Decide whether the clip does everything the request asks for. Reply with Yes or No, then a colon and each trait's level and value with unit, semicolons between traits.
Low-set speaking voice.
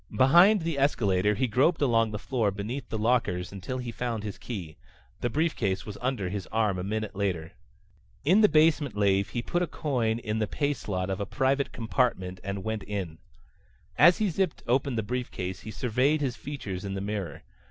Yes: low, 110 Hz